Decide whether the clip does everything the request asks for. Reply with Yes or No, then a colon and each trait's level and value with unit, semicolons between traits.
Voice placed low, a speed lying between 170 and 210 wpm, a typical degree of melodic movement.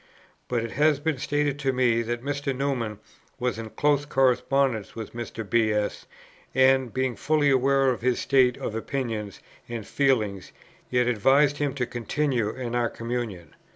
No: low, 125 Hz; average, 160 wpm; average, 3.1 semitones